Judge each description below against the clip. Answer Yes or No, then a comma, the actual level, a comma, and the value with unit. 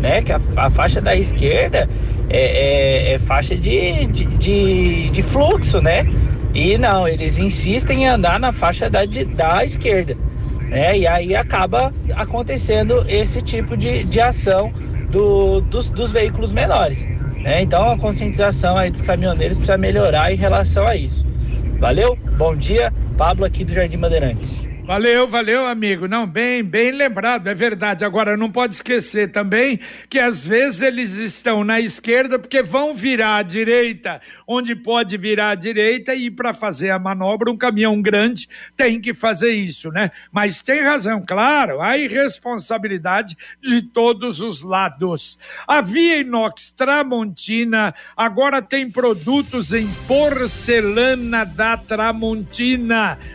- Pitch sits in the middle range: No, high, 225 Hz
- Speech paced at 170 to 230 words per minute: No, average, 145 wpm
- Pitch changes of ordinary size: Yes, average, 3.7 semitones